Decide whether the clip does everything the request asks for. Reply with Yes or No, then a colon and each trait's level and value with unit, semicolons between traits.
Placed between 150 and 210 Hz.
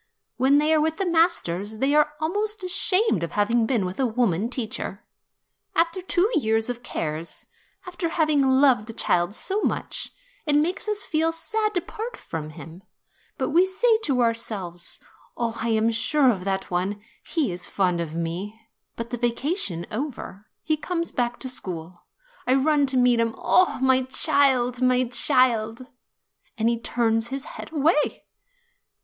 No: very high, 250 Hz